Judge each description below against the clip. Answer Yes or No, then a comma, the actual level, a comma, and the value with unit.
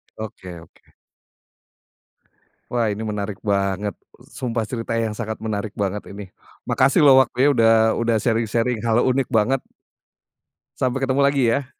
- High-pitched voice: No, low, 115 Hz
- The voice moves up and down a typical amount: Yes, average, 3.3 semitones